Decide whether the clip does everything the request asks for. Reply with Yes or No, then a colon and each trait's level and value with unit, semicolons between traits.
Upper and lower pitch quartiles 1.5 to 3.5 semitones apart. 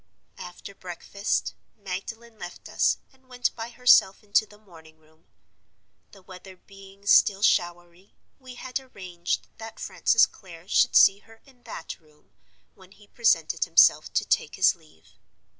No: average, 4.3 semitones